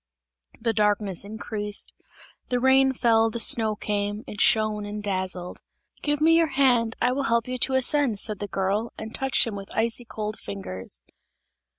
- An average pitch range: Yes, average, 3.2 semitones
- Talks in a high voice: Yes, high, 220 Hz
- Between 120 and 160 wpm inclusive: No, average, 170 wpm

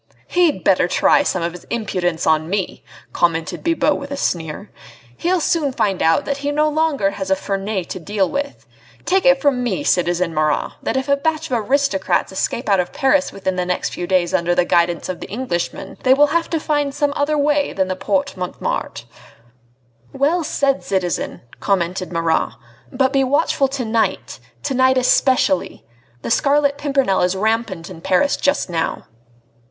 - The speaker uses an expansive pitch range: Yes, wide, 7.8 semitones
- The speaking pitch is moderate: No, high, 225 Hz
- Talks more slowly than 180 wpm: No, average, 185 wpm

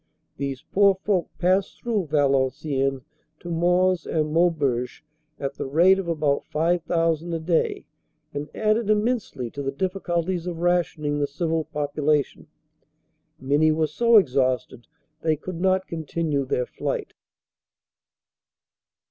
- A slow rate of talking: Yes, slow, 125 wpm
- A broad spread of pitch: No, average, 4.0 semitones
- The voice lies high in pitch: No, medium, 160 Hz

